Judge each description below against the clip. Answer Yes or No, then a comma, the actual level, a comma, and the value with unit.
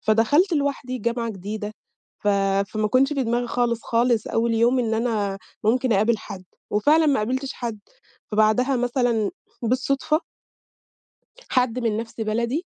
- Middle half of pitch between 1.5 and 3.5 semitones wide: Yes, average, 2.9 semitones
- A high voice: Yes, high, 235 Hz